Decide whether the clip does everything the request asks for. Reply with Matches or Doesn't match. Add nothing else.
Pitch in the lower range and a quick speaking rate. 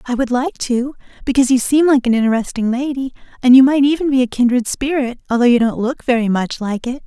Doesn't match